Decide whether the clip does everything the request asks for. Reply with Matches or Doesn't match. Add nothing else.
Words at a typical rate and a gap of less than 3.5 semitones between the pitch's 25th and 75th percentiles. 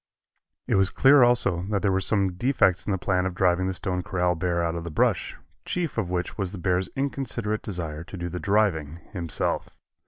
Doesn't match